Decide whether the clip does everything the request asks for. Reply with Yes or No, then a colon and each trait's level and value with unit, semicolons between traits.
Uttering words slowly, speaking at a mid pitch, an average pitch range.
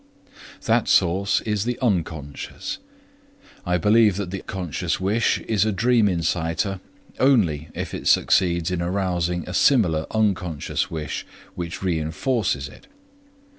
No: slow, 125 wpm; very low, 90 Hz; average, 4.1 semitones